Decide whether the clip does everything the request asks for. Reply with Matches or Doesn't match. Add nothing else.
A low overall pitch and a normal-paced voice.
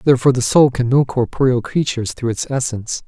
Matches